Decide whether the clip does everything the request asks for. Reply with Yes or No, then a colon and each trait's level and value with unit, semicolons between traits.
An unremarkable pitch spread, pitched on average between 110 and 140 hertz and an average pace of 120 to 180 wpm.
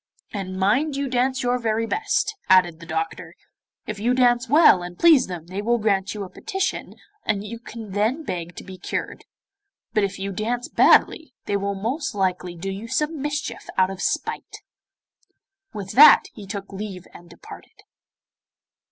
No: average, 4.8 semitones; high, 210 Hz; average, 170 wpm